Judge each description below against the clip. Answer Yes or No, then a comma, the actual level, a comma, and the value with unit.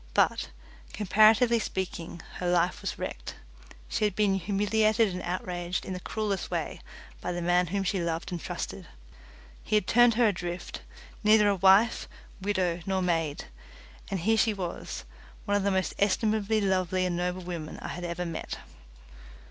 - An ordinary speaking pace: Yes, average, 165 wpm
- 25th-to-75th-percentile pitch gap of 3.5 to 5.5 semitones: No, average, 3.0 semitones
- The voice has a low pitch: No, high, 190 Hz